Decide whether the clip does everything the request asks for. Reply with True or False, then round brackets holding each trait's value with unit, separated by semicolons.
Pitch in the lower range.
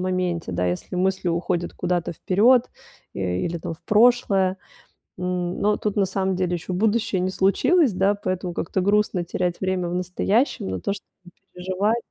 False (185 Hz)